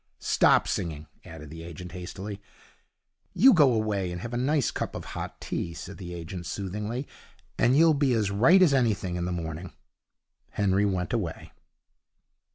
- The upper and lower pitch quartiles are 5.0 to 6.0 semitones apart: Yes, wide, 5.5 semitones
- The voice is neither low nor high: No, low, 100 Hz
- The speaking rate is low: No, average, 165 wpm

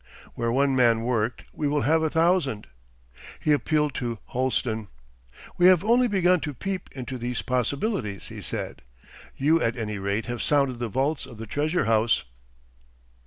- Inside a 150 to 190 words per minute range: Yes, average, 165 wpm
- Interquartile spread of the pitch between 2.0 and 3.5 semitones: No, average, 5.1 semitones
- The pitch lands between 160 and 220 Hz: No, low, 130 Hz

